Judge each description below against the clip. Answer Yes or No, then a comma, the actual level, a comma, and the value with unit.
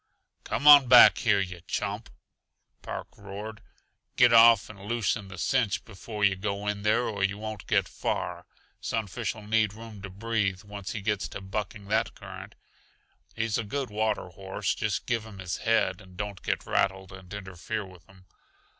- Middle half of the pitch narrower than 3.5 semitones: Yes, narrow, 2.4 semitones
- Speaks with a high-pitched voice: No, low, 105 Hz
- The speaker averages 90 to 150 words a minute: No, average, 170 wpm